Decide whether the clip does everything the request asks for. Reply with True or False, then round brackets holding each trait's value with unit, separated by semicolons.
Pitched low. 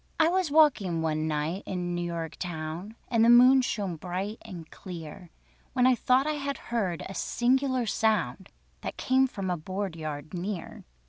False (190 Hz)